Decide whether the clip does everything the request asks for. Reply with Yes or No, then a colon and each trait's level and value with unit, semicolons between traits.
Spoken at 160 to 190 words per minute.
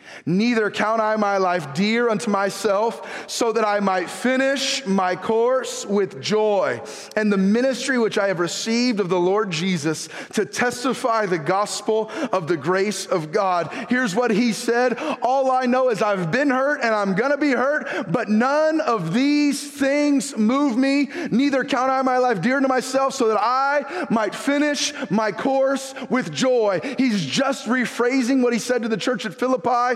Yes: average, 175 wpm